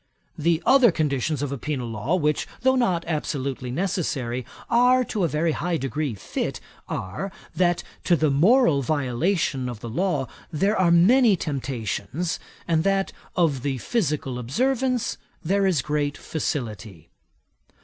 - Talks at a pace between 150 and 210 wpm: No, average, 140 wpm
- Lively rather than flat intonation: Yes, wide, 6.0 semitones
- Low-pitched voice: No, medium, 155 Hz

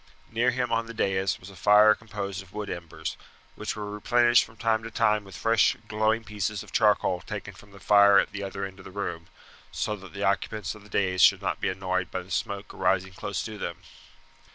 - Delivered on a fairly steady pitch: Yes, narrow, 2.3 semitones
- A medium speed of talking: No, fast, 225 wpm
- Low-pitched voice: Yes, low, 100 Hz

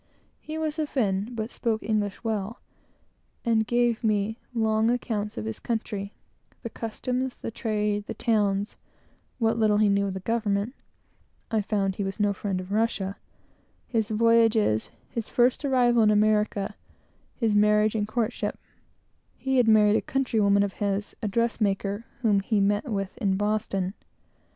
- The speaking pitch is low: No, high, 215 Hz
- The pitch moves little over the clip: Yes, narrow, 2.3 semitones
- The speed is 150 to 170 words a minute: Yes, average, 160 wpm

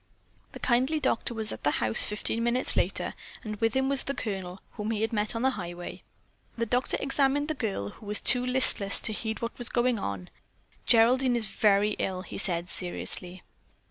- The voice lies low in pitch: No, high, 225 Hz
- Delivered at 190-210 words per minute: Yes, average, 195 wpm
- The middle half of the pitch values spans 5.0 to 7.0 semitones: No, average, 4.1 semitones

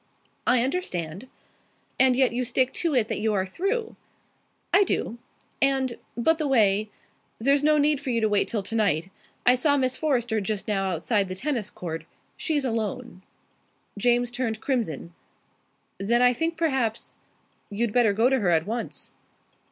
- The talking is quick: No, average, 165 wpm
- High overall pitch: Yes, high, 240 Hz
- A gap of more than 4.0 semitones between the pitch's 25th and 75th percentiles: Yes, average, 4.5 semitones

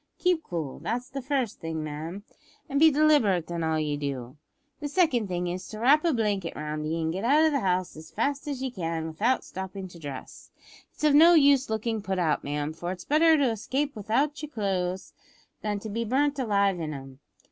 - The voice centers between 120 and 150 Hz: No, high, 205 Hz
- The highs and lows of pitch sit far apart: Yes, wide, 9.0 semitones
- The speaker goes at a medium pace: No, fast, 210 wpm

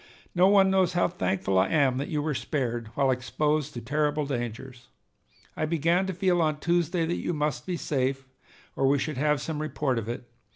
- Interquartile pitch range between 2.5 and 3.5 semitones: No, average, 4.3 semitones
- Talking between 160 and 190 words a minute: No, average, 200 wpm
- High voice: No, medium, 150 Hz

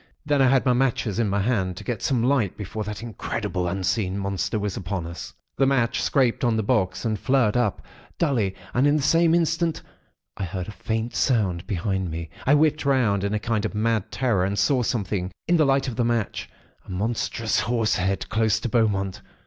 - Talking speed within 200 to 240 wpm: Yes, fast, 205 wpm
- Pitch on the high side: No, low, 110 Hz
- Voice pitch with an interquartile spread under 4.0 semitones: No, average, 4.5 semitones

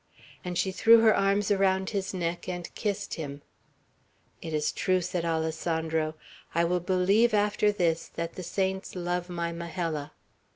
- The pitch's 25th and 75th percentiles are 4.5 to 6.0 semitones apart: No, average, 2.7 semitones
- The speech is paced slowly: No, average, 155 wpm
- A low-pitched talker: No, medium, 180 Hz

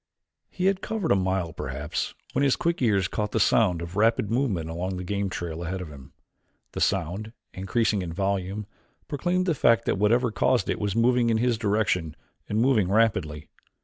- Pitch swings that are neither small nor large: Yes, average, 4.5 semitones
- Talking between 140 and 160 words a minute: No, average, 185 wpm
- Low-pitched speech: Yes, low, 105 Hz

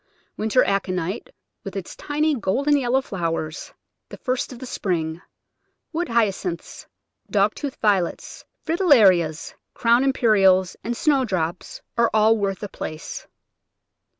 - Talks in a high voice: Yes, high, 210 Hz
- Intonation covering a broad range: Yes, wide, 5.8 semitones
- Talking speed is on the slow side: Yes, slow, 125 wpm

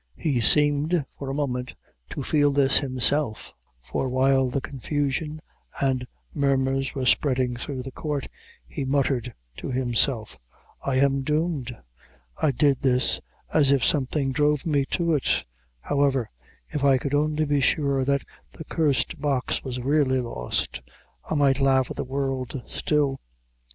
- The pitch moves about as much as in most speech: No, narrow, 2.0 semitones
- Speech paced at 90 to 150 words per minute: Yes, average, 145 wpm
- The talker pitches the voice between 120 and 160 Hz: Yes, low, 135 Hz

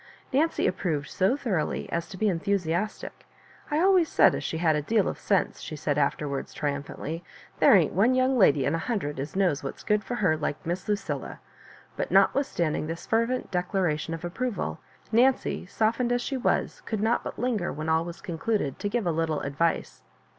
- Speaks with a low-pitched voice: No, medium, 185 Hz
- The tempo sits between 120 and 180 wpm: No, average, 190 wpm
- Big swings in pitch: Yes, wide, 6.3 semitones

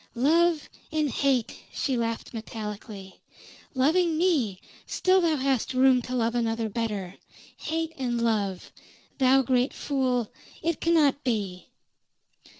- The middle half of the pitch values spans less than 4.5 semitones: No, average, 4.9 semitones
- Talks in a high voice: Yes, very high, 255 Hz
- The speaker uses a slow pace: Yes, slow, 120 wpm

